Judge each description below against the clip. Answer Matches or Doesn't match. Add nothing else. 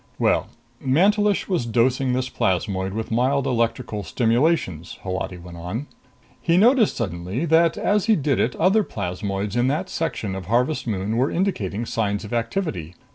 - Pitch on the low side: Matches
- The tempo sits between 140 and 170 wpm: Matches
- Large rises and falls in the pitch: Matches